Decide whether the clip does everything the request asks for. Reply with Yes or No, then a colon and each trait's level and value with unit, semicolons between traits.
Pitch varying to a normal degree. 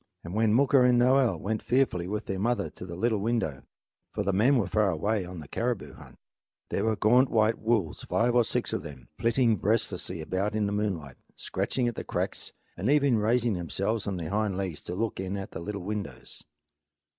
Yes: average, 3.8 semitones